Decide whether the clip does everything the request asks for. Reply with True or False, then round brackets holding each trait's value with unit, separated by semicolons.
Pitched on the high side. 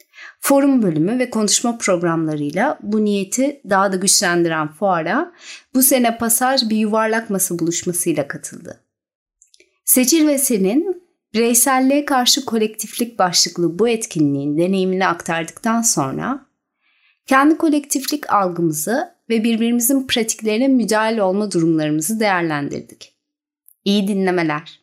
True (220 Hz)